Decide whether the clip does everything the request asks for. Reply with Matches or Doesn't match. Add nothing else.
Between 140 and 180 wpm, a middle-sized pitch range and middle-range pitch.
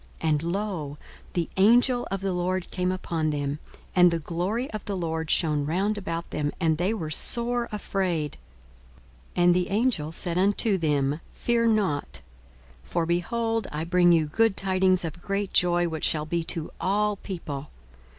Matches